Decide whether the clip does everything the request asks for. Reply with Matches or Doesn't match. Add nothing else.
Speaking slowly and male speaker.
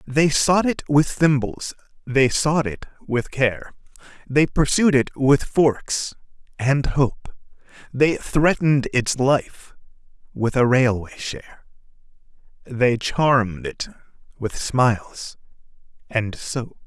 Matches